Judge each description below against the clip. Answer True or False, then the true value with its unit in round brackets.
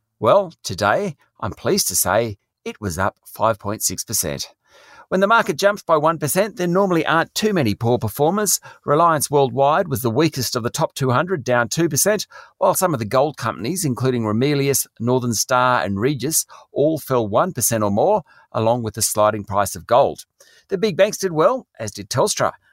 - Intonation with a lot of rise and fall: True (6.9 semitones)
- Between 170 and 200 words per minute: True (175 wpm)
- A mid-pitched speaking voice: False (130 Hz)